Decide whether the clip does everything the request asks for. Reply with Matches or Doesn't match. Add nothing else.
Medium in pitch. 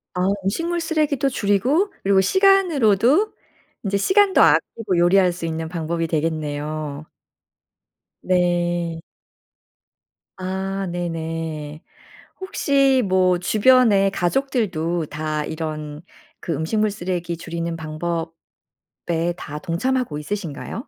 Matches